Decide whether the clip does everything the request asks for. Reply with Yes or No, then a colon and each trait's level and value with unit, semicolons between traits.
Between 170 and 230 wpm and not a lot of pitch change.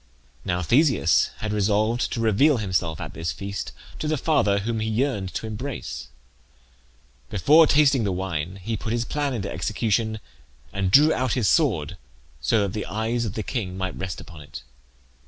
No: average, 175 wpm; average, 4.3 semitones